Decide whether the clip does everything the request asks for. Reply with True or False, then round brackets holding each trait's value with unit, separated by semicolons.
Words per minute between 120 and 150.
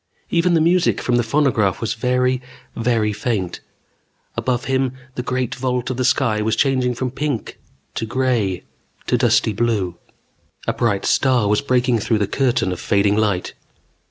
False (160 wpm)